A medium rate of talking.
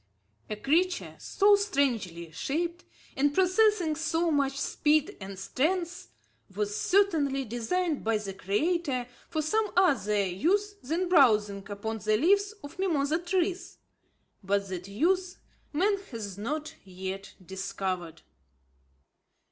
No: slow, 115 wpm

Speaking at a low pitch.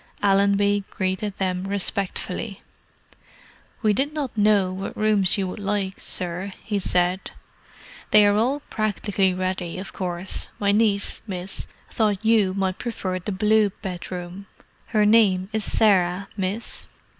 No: high, 200 Hz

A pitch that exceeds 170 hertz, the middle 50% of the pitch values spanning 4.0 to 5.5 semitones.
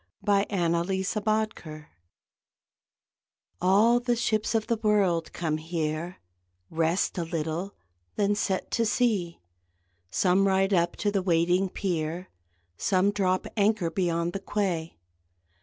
No: medium, 185 Hz; average, 3.4 semitones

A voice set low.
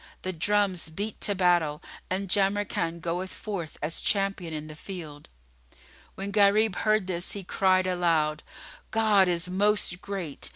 No: medium, 185 Hz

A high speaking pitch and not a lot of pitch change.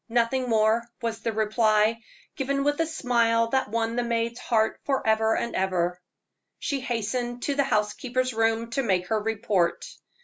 Yes: high, 230 Hz; narrow, 2.3 semitones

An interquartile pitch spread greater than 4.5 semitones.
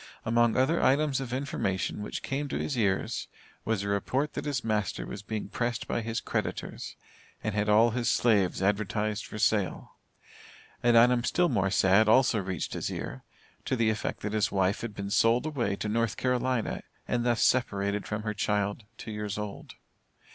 No: average, 3.1 semitones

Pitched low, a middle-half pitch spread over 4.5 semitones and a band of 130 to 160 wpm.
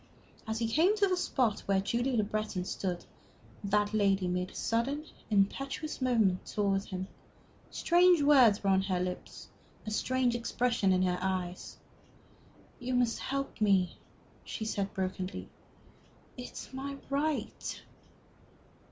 No: high, 215 Hz; average, 5.2 semitones; slow, 135 wpm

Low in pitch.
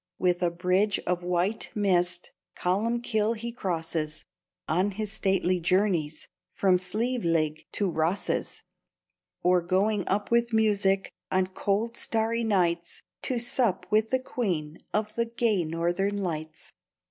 No: high, 195 Hz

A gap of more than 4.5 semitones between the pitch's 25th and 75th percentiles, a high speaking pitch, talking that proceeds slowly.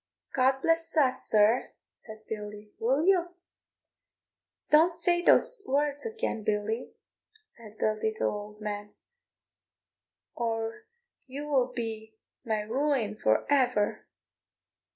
Yes: wide, 5.5 semitones; high, 240 Hz; slow, 110 wpm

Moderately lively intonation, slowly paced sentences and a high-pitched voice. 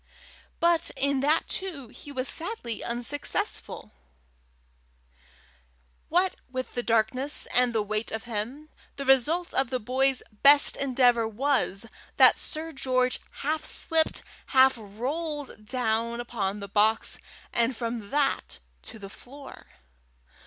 Yes: average, 4.0 semitones; slow, 125 wpm; very high, 255 Hz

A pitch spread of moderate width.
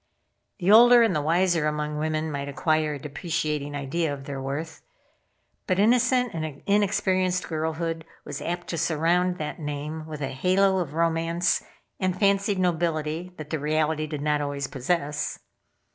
Yes: average, 3.3 semitones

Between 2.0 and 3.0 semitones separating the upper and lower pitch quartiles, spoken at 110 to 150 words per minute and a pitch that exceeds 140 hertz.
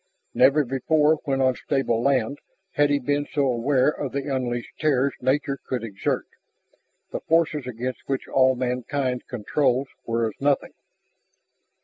No: narrow, 2.4 semitones; average, 140 wpm; low, 135 Hz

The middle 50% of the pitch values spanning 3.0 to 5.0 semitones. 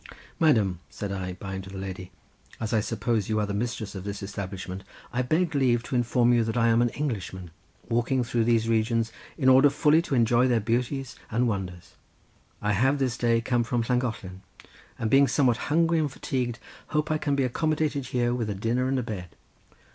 Yes: average, 3.8 semitones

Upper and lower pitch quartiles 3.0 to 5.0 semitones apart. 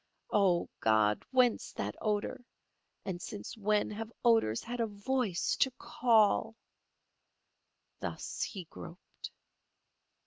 Yes: average, 4.7 semitones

